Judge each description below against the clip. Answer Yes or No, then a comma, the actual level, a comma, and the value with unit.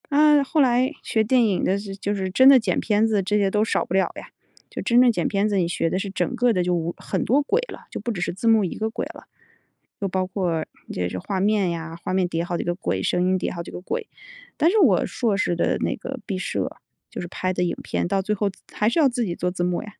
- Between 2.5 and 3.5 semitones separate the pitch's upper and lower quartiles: No, average, 4.5 semitones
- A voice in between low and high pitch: No, high, 195 Hz